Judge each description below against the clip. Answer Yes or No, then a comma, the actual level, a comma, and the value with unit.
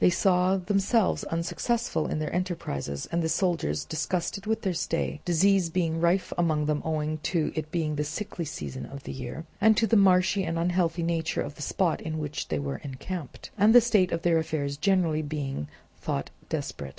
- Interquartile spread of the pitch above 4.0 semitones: No, average, 3.4 semitones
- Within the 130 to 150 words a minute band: No, average, 190 wpm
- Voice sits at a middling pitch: Yes, medium, 165 Hz